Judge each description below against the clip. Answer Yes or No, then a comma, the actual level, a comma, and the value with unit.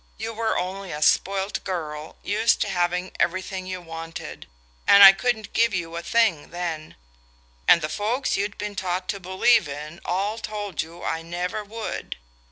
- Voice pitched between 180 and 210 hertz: Yes, medium, 185 Hz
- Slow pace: No, average, 170 wpm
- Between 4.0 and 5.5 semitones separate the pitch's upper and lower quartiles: No, average, 3.5 semitones